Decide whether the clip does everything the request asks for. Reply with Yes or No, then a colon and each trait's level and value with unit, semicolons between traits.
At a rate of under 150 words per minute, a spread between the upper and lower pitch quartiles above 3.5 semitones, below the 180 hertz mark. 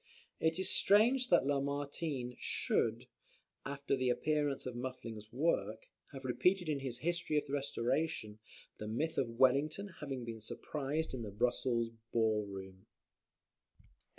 Yes: average, 140 wpm; average, 4.7 semitones; low, 135 Hz